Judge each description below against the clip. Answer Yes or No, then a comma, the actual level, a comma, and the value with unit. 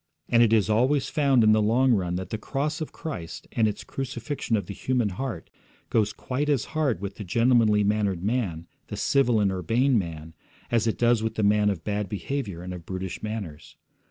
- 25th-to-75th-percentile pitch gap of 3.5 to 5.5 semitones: Yes, average, 4.4 semitones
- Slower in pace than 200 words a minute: No, fast, 205 wpm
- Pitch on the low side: Yes, low, 110 Hz